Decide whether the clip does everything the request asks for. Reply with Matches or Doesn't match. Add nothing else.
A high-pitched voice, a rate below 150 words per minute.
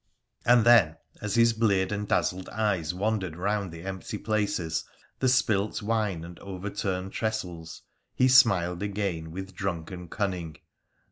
Doesn't match